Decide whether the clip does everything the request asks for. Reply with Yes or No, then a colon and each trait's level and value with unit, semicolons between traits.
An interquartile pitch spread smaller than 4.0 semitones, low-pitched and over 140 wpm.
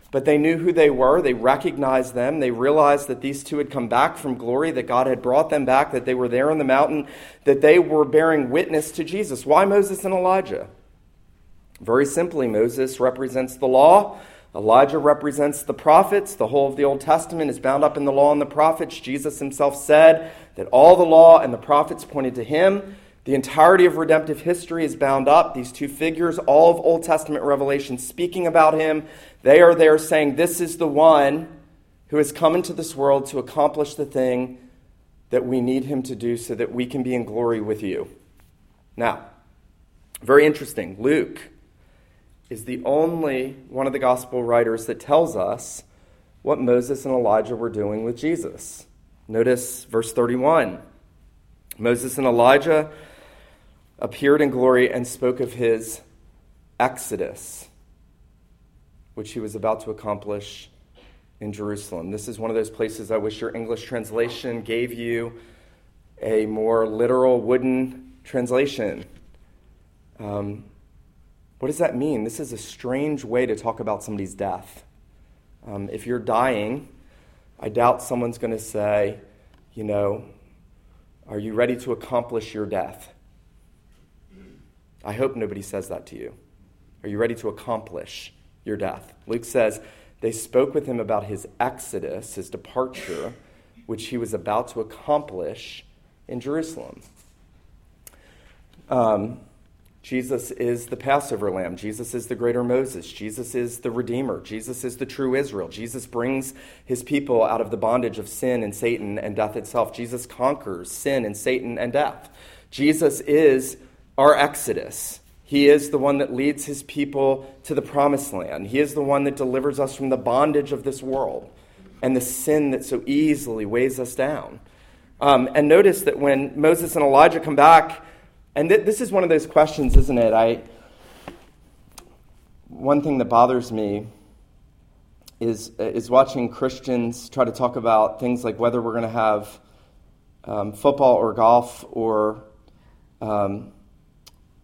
No: average, 4.8 semitones; low, 125 Hz; average, 160 wpm